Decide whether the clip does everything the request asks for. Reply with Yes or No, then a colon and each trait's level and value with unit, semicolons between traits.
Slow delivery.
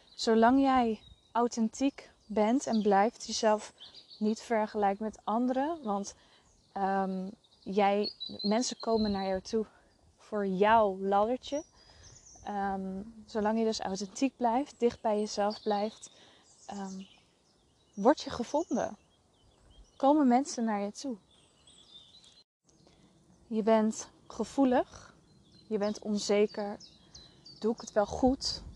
Yes: slow, 110 wpm